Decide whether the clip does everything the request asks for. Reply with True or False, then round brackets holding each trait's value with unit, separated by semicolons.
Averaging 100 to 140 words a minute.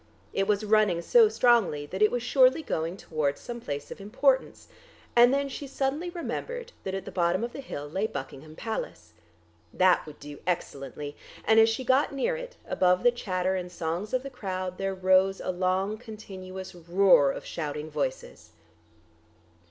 False (175 wpm)